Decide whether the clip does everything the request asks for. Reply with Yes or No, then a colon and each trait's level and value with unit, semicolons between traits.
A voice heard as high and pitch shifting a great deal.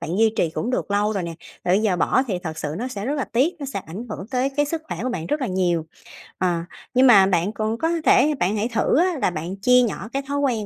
Yes: high, 215 Hz; wide, 6.0 semitones